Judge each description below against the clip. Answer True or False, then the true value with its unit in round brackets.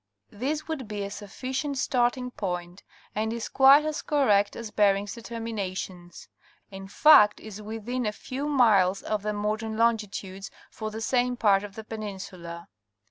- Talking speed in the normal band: True (150 wpm)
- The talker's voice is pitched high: True (215 Hz)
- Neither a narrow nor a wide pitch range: True (3.6 semitones)